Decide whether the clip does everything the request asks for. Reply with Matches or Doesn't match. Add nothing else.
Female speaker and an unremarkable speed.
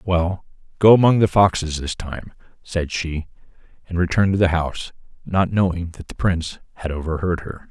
Doesn't match